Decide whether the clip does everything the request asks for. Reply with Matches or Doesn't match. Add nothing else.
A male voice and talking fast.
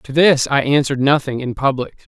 Doesn't match